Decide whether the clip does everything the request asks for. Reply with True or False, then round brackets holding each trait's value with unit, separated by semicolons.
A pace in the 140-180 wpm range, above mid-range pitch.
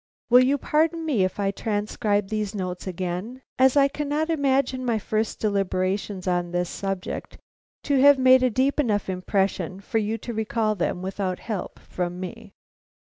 True (165 wpm; 215 Hz)